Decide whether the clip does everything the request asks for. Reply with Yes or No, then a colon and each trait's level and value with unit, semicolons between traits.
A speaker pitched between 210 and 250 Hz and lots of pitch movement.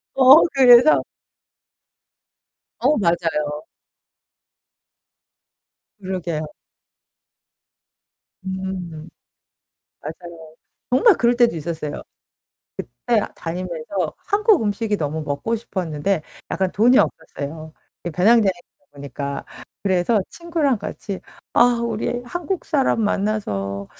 No: high, 190 Hz; wide, 6.9 semitones